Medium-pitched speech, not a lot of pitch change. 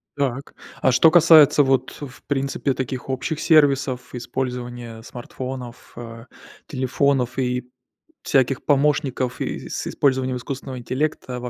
No: low, 130 Hz; narrow, 2.0 semitones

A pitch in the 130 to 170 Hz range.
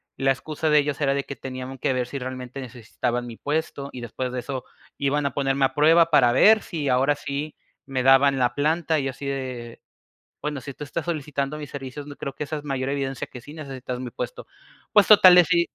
Yes: medium, 140 Hz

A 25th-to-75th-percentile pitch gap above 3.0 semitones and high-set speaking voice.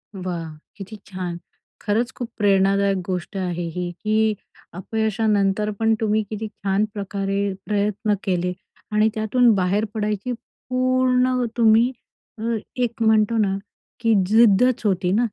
No: narrow, 2.6 semitones; high, 210 Hz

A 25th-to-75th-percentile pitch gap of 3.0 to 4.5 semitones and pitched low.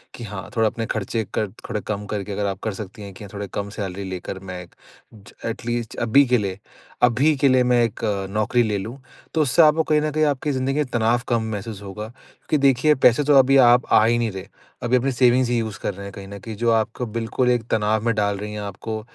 Yes: average, 3.5 semitones; low, 115 Hz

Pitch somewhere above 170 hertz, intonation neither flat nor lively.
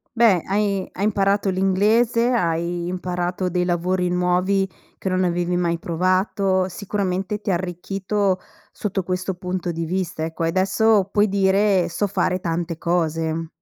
No: medium, 185 Hz; narrow, 2.0 semitones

